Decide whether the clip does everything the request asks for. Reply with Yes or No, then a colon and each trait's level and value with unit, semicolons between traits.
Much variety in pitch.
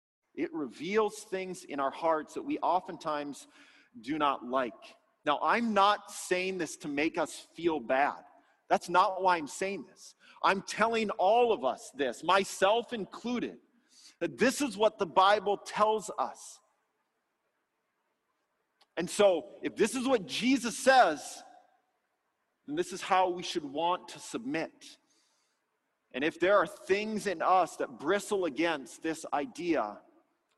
Yes: wide, 6.7 semitones